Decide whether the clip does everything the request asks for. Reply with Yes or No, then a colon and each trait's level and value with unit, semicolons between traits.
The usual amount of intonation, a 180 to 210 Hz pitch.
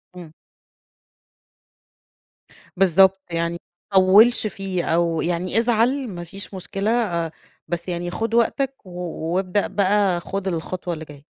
Yes: average, 3.2 semitones; medium, 185 Hz